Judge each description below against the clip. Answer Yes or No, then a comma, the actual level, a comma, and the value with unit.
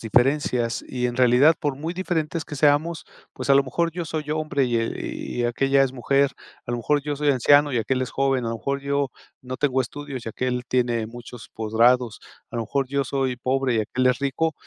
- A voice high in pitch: No, low, 135 Hz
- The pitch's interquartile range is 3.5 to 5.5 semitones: No, average, 2.9 semitones